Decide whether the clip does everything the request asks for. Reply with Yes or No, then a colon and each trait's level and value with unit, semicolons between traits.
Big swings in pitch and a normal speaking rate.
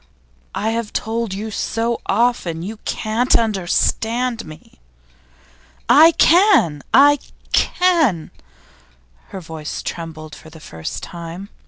No: wide, 6.3 semitones; slow, 110 wpm